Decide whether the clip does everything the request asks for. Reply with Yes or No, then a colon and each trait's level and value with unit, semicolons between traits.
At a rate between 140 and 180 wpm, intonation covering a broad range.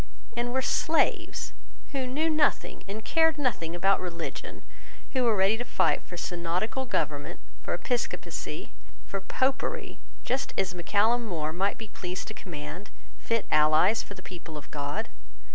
Yes: average, 155 wpm; wide, 6.0 semitones